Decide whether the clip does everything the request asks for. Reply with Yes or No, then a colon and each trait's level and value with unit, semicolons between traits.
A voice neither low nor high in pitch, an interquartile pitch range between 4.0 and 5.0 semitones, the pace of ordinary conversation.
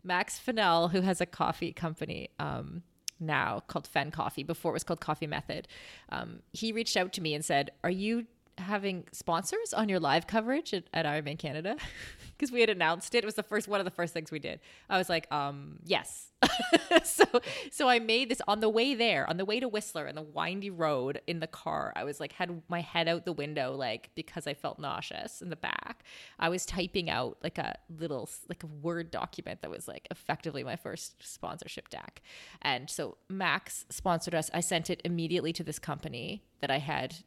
No: medium, 175 Hz; average, 4.6 semitones; fast, 210 wpm